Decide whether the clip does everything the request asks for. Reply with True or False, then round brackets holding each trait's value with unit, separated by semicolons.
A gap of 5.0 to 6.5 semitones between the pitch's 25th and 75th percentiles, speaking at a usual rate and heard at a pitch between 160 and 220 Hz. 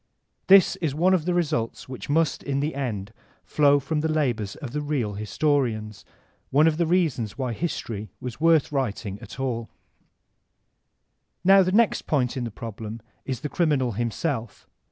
False (5.5 semitones; 170 wpm; 135 Hz)